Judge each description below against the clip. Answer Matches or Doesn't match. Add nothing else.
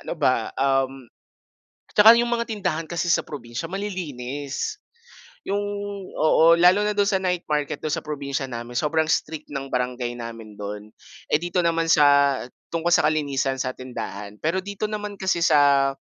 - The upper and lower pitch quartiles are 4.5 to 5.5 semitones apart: Matches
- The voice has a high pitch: Doesn't match